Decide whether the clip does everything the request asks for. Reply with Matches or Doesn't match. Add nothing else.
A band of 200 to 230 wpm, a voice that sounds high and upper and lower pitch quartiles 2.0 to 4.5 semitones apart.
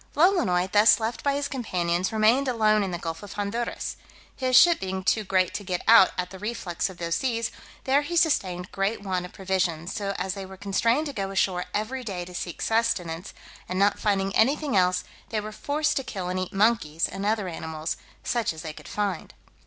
Matches